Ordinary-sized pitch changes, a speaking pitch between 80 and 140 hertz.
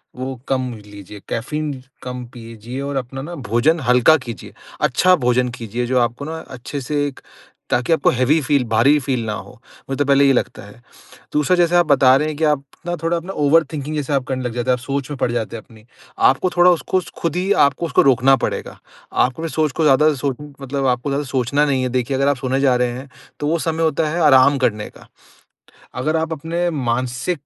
Yes: average, 3.5 semitones; low, 135 Hz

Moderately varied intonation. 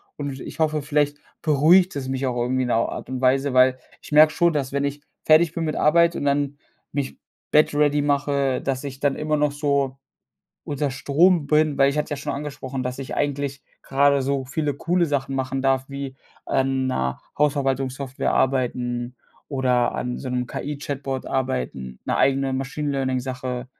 No: narrow, 2.0 semitones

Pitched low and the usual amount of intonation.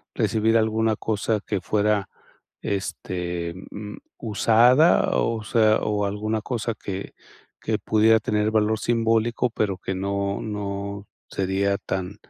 No: low, 105 Hz; narrow, 2.0 semitones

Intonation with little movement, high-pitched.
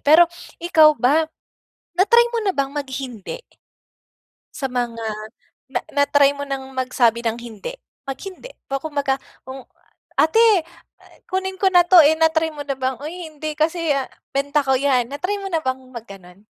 No: average, 4.1 semitones; very high, 285 Hz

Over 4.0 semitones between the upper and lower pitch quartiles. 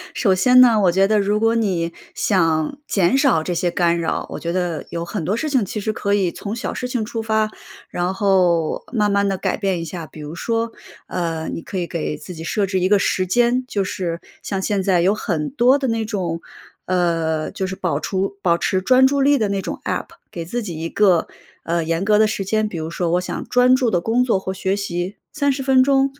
Yes: average, 4.5 semitones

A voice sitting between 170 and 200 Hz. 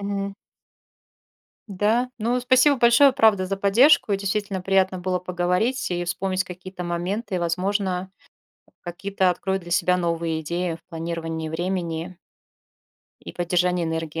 Yes: medium, 185 Hz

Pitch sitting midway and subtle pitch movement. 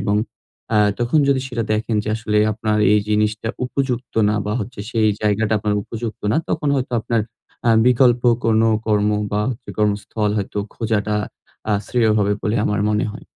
No: low, 110 Hz; narrow, 2.0 semitones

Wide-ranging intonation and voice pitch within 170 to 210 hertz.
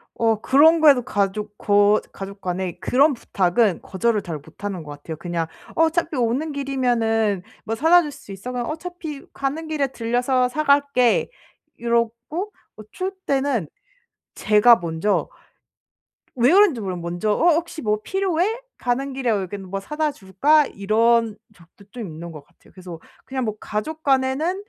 No: wide, 6.4 semitones; high, 235 Hz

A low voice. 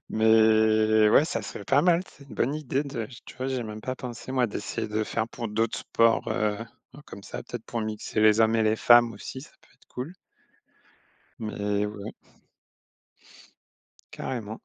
Yes: low, 110 Hz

